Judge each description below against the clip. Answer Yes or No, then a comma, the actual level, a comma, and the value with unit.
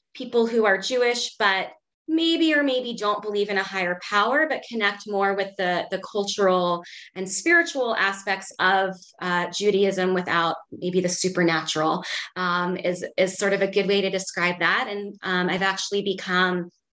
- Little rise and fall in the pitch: Yes, narrow, 2.3 semitones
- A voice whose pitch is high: Yes, high, 195 Hz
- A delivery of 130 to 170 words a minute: Yes, average, 165 wpm